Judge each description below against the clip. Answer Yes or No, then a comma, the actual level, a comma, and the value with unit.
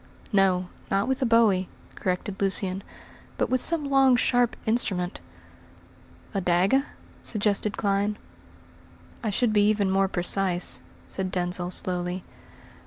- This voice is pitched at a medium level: No, high, 195 Hz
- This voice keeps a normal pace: No, slow, 120 wpm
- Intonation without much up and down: No, average, 3.8 semitones